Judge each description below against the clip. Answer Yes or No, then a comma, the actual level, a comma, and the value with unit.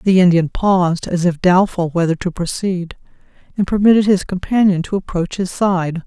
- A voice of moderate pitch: Yes, medium, 180 Hz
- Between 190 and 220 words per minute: No, average, 170 wpm